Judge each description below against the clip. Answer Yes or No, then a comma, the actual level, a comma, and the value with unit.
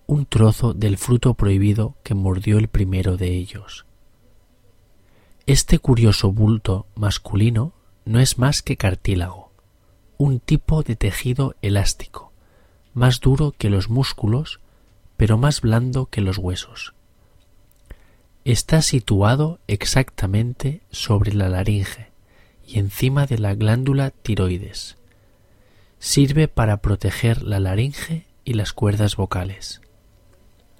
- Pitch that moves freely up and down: No, average, 4.1 semitones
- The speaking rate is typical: No, slow, 110 wpm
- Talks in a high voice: No, low, 105 Hz